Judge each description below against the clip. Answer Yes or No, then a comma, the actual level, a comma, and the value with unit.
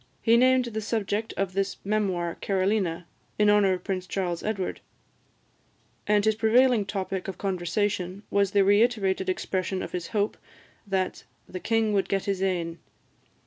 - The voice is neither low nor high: No, high, 195 Hz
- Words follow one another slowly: No, average, 150 wpm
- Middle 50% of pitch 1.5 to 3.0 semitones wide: Yes, narrow, 2.4 semitones